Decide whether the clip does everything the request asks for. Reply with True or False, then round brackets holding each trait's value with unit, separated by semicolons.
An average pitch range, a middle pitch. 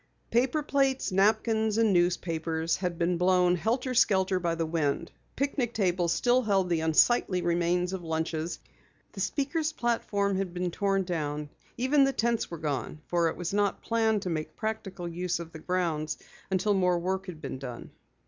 True (4.6 semitones; 180 Hz)